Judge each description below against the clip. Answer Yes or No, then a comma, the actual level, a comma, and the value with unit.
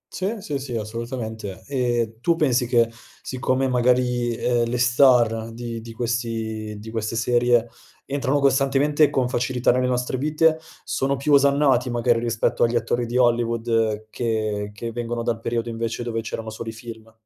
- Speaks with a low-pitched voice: Yes, low, 120 Hz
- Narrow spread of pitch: Yes, narrow, 2.0 semitones